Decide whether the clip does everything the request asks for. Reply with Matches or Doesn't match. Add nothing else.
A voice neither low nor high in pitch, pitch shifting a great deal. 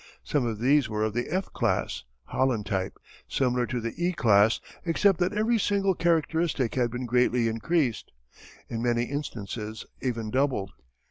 Doesn't match